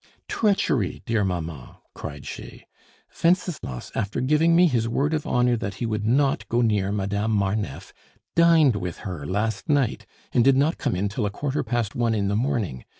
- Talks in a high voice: No, low, 115 Hz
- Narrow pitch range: No, wide, 5.5 semitones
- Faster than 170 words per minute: Yes, average, 180 wpm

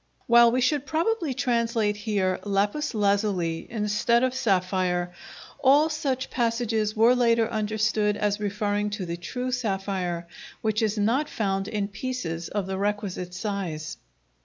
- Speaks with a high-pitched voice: Yes, high, 210 Hz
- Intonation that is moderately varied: Yes, average, 3.4 semitones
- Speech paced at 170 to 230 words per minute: No, slow, 135 wpm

